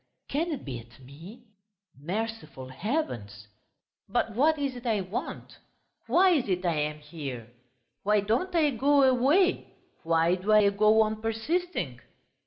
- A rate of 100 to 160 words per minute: Yes, average, 145 wpm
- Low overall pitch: No, high, 215 Hz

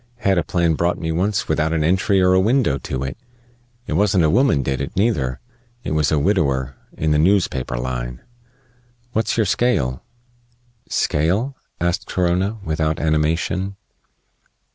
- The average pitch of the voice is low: Yes, very low, 85 Hz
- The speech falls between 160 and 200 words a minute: No, average, 150 wpm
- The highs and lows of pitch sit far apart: No, average, 4.8 semitones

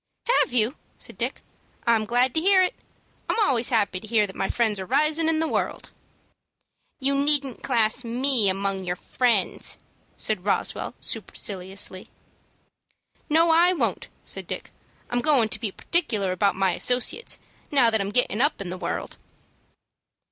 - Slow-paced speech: No, average, 155 wpm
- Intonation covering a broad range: Yes, wide, 6.0 semitones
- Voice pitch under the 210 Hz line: No, high, 235 Hz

